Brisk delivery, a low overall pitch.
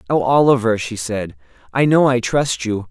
No: average, 185 wpm; low, 115 Hz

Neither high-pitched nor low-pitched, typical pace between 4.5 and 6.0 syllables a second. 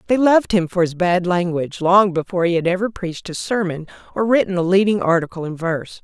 No: medium, 180 Hz; 6.3 syllables/s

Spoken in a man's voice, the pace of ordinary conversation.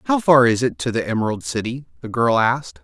No: male; fast, 235 wpm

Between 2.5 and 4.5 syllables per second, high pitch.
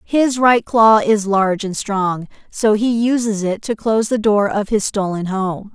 Yes: 4.2 syllables/s; high, 210 Hz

